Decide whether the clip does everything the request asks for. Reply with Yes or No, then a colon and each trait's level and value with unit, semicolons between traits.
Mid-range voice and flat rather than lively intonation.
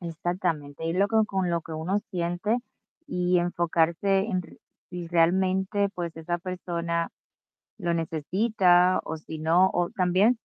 Yes: medium, 175 Hz; narrow, 2.0 semitones